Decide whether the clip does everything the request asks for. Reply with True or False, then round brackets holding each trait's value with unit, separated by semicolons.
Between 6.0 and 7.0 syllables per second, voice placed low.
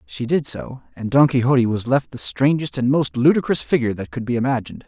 True (6.1 syllables/s; 125 Hz)